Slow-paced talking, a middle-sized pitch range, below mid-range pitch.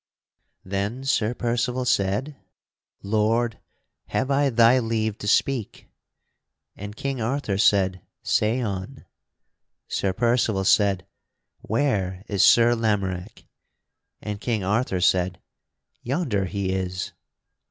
Yes: slow, 105 wpm; average, 3.8 semitones; low, 110 Hz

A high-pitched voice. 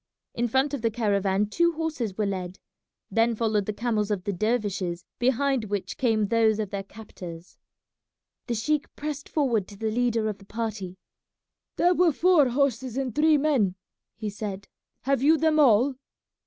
Yes: high, 225 Hz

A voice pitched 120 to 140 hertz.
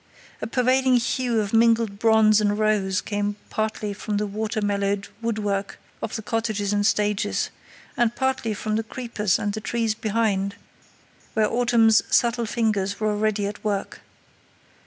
No: high, 215 Hz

